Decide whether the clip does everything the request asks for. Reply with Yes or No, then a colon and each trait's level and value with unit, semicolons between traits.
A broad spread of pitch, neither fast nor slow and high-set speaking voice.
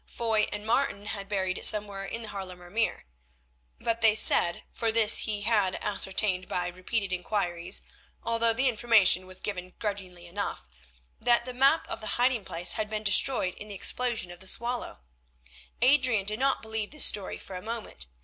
No: average, 3.6 semitones; average, 180 wpm; high, 210 Hz